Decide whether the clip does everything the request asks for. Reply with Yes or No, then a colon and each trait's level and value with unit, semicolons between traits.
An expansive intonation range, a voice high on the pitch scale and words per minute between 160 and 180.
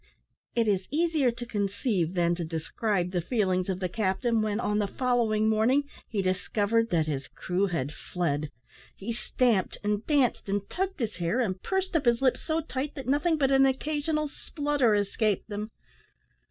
Yes: wide, 5.9 semitones; high, 220 Hz; average, 175 wpm